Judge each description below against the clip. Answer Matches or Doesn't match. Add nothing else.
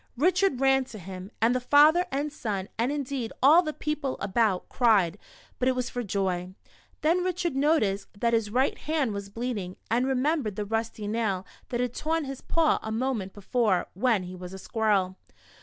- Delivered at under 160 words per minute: Doesn't match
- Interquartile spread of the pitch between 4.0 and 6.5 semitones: Matches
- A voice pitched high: Matches